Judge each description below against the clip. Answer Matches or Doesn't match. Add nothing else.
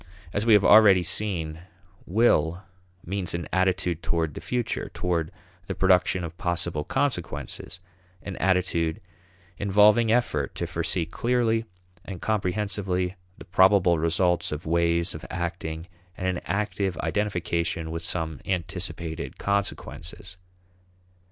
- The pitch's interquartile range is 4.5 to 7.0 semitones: Doesn't match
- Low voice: Matches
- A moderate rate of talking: Doesn't match